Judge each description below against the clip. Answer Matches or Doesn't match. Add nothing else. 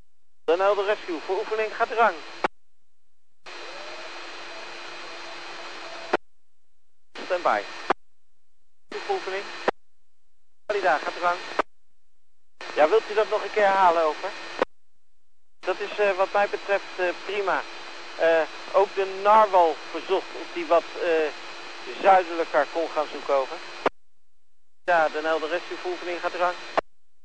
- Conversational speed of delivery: Doesn't match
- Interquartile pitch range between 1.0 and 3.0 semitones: Doesn't match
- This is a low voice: Doesn't match